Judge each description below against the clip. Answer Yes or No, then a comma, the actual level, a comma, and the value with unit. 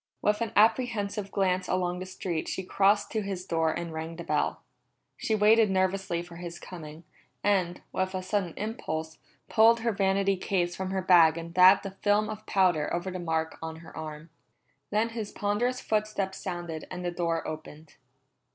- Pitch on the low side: No, medium, 185 Hz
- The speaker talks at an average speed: Yes, average, 180 wpm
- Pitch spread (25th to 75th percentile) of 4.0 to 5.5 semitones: No, average, 3.3 semitones